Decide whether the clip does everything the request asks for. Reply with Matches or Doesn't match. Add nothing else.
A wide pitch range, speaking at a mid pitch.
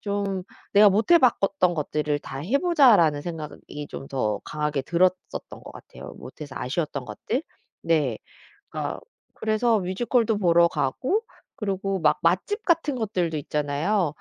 Matches